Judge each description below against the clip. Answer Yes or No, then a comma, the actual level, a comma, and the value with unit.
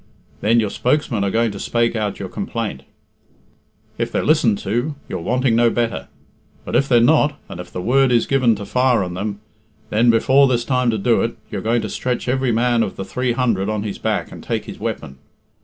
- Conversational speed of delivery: No, fast, 215 wpm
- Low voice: Yes, low, 115 Hz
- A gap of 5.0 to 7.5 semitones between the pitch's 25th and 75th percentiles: No, average, 3.2 semitones